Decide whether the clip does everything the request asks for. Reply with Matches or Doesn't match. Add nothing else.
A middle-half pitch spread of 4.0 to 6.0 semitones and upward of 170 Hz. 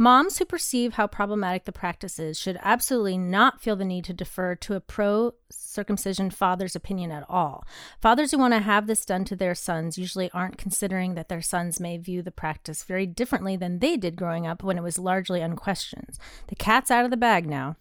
Doesn't match